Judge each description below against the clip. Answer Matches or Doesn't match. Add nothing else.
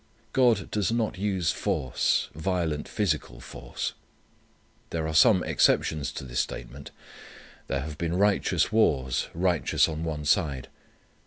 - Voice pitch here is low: Matches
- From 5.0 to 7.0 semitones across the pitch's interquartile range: Matches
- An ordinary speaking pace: Doesn't match